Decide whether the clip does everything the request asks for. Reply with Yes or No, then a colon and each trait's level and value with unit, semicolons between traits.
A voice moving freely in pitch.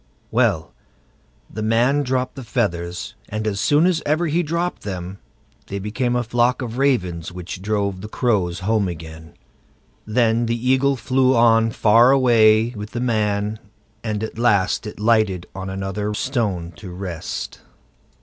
No: average, 4.1 semitones